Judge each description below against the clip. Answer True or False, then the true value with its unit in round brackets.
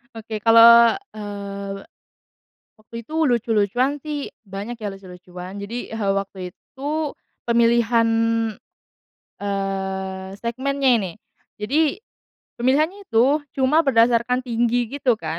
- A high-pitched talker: True (230 Hz)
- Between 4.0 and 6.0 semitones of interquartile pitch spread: True (4.3 semitones)